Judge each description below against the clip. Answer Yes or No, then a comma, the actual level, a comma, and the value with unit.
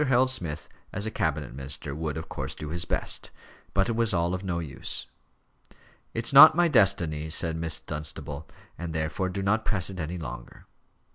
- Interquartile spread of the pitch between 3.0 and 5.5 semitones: Yes, average, 4.6 semitones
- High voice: No, very low, 85 Hz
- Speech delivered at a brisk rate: No, average, 185 wpm